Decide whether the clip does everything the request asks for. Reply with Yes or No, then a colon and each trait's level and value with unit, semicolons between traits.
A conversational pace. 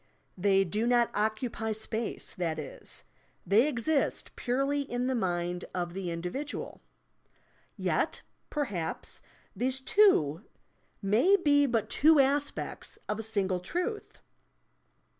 No: slow, 115 wpm